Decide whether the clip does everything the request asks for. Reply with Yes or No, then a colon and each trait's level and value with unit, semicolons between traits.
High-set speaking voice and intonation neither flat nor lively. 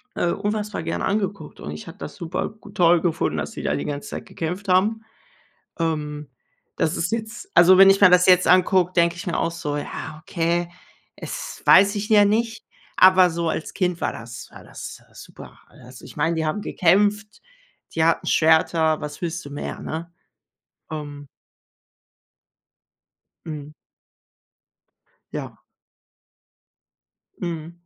No: medium, 170 Hz; average, 3.5 semitones